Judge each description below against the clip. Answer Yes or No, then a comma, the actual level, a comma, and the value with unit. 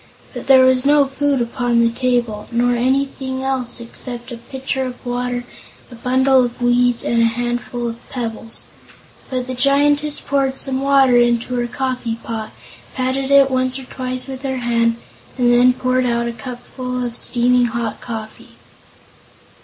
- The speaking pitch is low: No, very high, 250 Hz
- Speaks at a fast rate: No, average, 160 wpm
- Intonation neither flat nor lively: No, narrow, 1.7 semitones